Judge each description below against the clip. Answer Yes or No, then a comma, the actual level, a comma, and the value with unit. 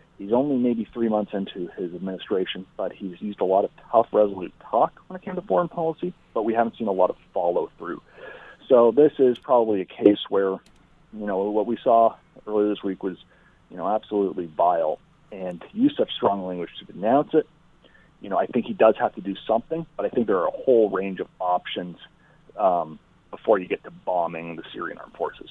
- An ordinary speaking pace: No, fast, 210 wpm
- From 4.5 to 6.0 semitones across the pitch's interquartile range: Yes, average, 4.9 semitones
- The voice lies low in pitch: Yes, low, 105 Hz